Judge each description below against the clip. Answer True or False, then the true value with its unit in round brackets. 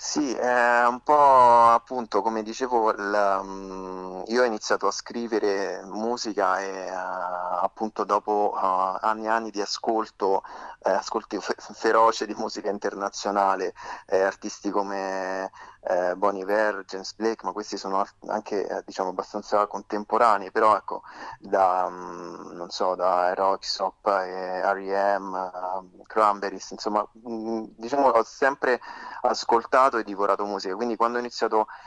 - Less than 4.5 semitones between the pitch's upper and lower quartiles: True (2.9 semitones)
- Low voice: True (100 Hz)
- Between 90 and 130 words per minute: True (120 wpm)